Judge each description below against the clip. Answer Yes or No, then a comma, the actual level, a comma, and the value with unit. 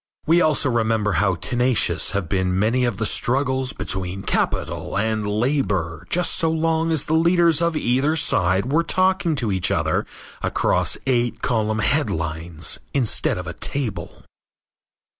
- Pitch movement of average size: No, wide, 7.7 semitones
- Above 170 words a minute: No, average, 145 wpm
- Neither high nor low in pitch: No, low, 120 Hz